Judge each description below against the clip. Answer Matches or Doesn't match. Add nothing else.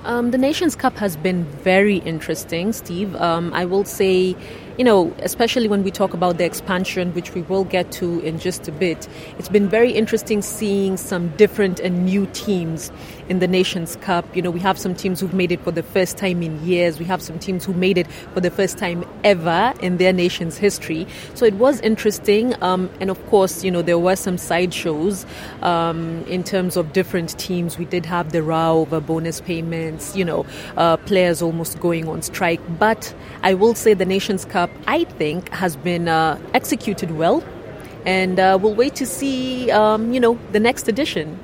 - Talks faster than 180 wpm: Matches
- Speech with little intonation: Doesn't match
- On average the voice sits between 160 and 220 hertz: Matches